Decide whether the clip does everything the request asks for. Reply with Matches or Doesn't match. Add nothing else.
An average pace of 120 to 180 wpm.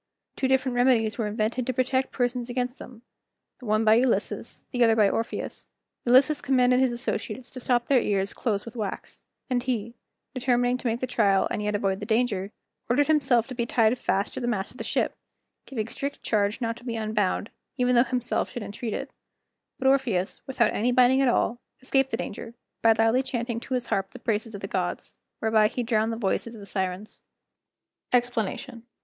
Doesn't match